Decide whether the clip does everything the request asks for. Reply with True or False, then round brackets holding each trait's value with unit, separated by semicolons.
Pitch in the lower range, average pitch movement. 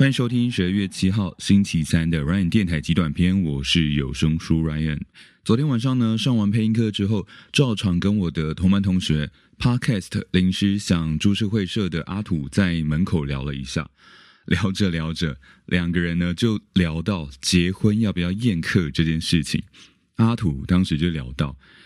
True (90 Hz; 4.4 semitones)